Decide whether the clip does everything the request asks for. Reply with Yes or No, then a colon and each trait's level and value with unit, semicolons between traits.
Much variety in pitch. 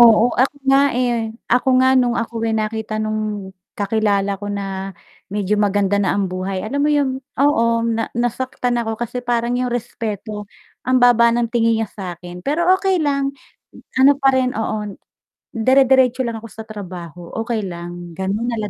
No: average, 3.6 semitones